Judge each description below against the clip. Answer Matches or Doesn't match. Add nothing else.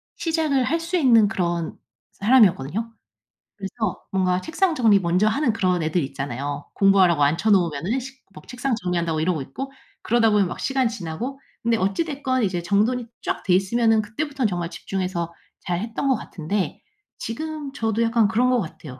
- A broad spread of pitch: Matches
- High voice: Matches